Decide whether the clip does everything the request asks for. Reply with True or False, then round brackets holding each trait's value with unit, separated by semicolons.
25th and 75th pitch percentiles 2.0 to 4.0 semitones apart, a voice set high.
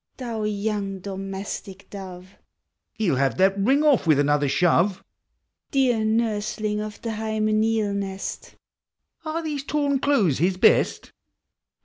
True (2.8 semitones; 210 Hz)